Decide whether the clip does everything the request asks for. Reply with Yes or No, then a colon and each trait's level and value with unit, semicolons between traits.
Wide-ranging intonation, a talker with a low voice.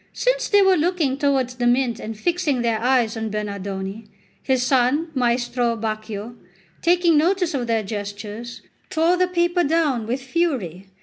No: wide, 6.8 semitones; very high, 250 Hz